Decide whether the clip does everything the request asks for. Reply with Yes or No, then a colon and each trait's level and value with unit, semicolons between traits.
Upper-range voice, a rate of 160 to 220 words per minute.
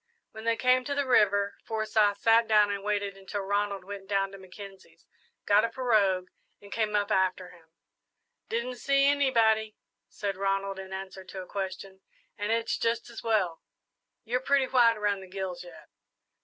Yes: high, 205 Hz; average, 170 wpm